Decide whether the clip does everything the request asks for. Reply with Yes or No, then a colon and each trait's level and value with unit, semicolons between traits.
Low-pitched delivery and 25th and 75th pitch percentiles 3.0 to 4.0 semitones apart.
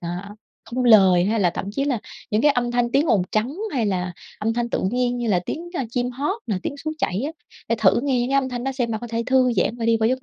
No: high, 240 Hz; average, 3.3 semitones